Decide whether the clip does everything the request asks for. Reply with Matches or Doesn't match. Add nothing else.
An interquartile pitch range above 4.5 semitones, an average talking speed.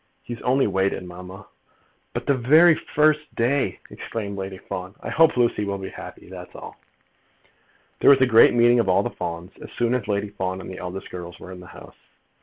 Doesn't match